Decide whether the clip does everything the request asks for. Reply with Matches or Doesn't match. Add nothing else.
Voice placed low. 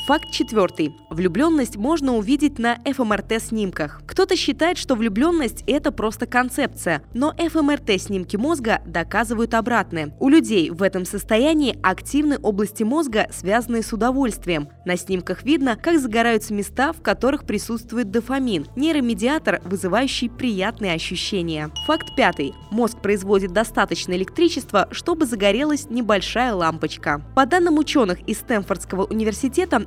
Doesn't match